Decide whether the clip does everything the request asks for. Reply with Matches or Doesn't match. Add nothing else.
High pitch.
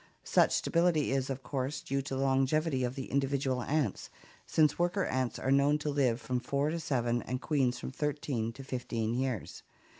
Doesn't match